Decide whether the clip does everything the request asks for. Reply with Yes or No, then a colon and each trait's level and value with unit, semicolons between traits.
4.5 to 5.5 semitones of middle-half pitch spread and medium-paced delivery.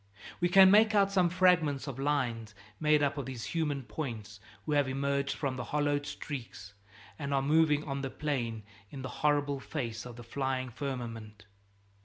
No: average, 3.4 semitones; average, 175 wpm